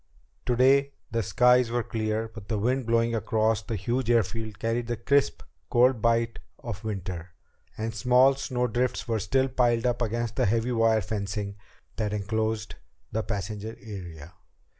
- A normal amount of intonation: No, narrow, 2.3 semitones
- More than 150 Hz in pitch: No, low, 115 Hz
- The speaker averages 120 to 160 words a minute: Yes, average, 150 wpm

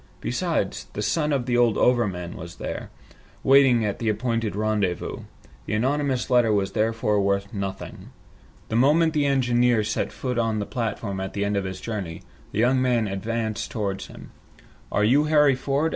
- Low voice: Yes, low, 115 Hz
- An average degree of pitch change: Yes, average, 3.9 semitones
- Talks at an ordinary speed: Yes, average, 175 wpm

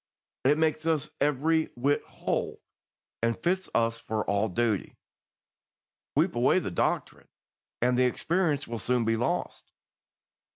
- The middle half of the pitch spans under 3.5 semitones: No, average, 5.2 semitones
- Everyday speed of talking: No, slow, 130 wpm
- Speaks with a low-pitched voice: Yes, low, 125 Hz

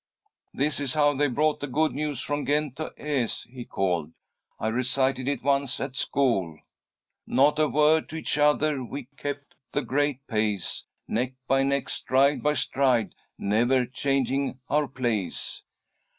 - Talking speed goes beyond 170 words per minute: No, average, 150 wpm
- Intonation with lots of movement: No, average, 2.8 semitones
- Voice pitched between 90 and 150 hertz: Yes, low, 135 Hz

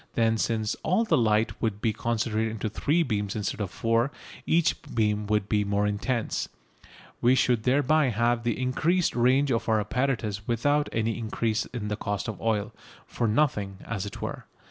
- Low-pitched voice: Yes, low, 115 Hz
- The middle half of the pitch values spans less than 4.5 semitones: Yes, average, 3.2 semitones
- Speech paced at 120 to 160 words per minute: No, average, 175 wpm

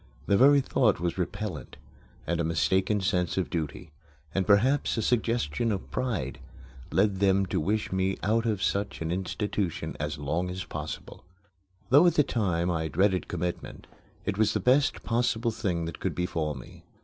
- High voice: No, very low, 95 Hz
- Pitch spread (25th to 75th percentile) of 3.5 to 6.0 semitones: Yes, average, 4.6 semitones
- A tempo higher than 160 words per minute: Yes, average, 170 wpm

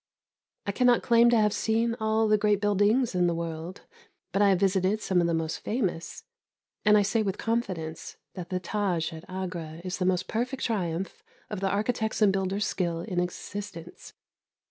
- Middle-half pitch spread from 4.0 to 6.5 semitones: No, average, 3.5 semitones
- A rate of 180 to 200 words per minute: Yes, average, 185 wpm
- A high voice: Yes, high, 195 Hz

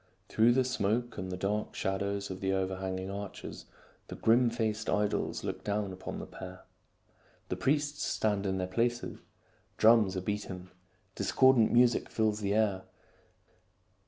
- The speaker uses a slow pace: No, average, 150 wpm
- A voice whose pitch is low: Yes, low, 105 Hz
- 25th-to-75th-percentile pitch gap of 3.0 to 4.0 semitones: Yes, average, 3.3 semitones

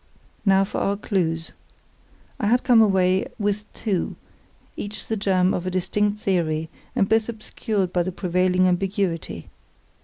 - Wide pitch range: No, narrow, 2.4 semitones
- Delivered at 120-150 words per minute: Yes, average, 145 wpm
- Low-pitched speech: No, high, 190 Hz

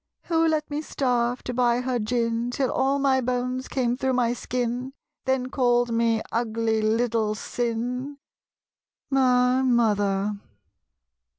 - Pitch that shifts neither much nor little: No, narrow, 2.0 semitones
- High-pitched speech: Yes, high, 245 Hz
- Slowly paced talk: Yes, slow, 125 wpm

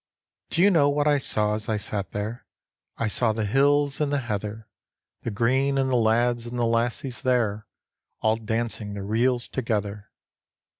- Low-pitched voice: Yes, low, 115 Hz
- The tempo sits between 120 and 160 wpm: No, average, 170 wpm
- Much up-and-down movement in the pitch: No, average, 3.5 semitones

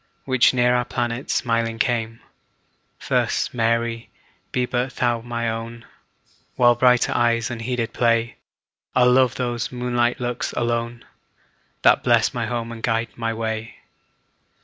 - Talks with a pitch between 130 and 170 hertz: No, low, 120 Hz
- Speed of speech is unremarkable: No, slow, 130 wpm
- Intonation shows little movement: Yes, narrow, 1.1 semitones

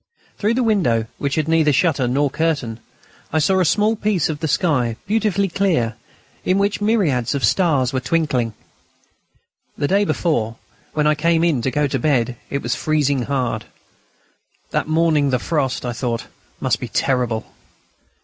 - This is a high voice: No, medium, 150 Hz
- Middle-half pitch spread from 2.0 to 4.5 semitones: No, average, 5.2 semitones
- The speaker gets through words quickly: No, average, 165 wpm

